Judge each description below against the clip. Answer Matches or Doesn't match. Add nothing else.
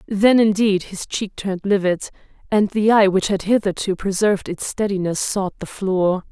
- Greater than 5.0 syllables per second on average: Doesn't match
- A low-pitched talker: Doesn't match